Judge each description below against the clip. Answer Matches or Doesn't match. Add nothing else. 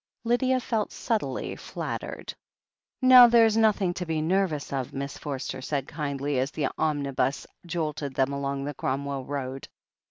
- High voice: Doesn't match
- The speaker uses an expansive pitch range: Matches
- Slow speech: Doesn't match